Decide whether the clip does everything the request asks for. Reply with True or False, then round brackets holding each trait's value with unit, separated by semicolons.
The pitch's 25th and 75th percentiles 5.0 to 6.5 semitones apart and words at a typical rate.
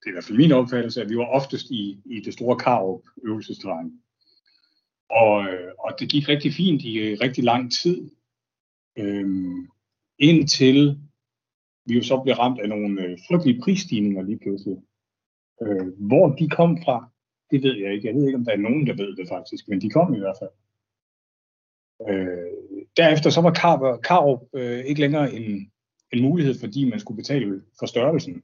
True (5.5 semitones; 175 wpm)